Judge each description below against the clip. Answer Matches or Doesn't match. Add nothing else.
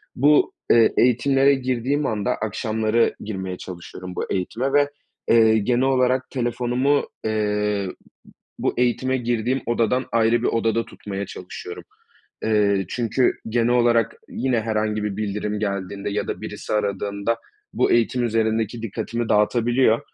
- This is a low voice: Matches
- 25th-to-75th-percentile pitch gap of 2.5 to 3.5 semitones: Matches